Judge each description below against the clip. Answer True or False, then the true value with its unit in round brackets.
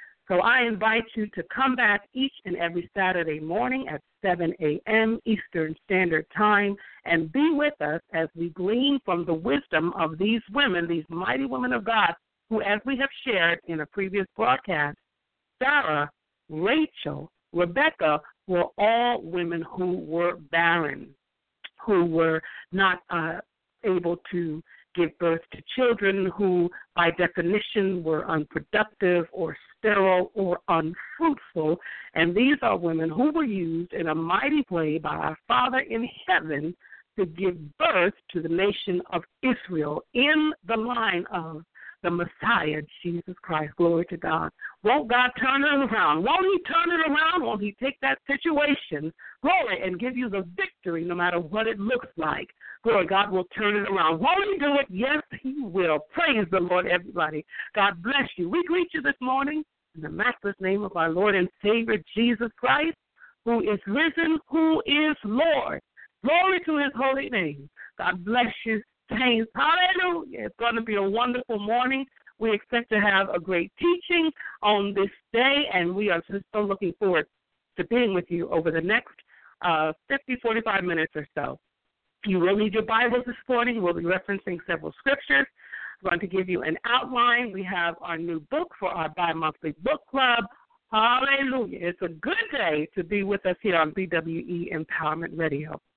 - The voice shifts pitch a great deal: True (6.5 semitones)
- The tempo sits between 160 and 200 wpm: True (170 wpm)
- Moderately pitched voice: False (200 Hz)